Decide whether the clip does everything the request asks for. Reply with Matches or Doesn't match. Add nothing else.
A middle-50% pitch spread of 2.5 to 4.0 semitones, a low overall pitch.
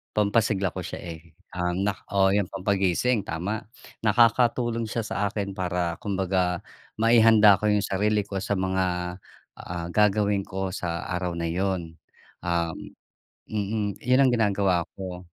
Matches